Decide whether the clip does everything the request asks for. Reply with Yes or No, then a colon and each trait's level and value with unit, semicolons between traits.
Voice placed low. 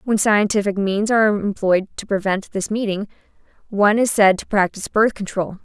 No: high, 205 Hz